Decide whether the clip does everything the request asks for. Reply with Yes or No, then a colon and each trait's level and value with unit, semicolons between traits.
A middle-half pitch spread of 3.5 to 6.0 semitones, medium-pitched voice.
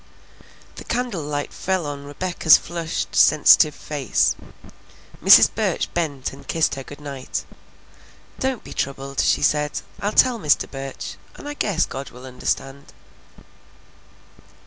Yes: average, 4.0 semitones; medium, 150 Hz